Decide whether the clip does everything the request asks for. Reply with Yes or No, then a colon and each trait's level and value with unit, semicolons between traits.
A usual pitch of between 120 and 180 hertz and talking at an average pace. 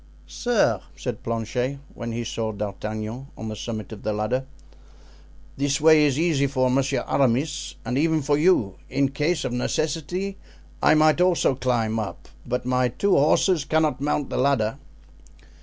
Yes: low, 135 Hz; average, 155 wpm